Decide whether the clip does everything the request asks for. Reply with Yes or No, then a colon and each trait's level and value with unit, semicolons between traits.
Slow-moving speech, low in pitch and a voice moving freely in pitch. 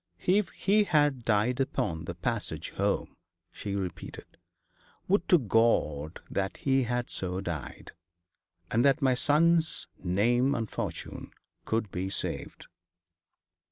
Yes: slow, 125 wpm; low, 120 Hz; wide, 6.5 semitones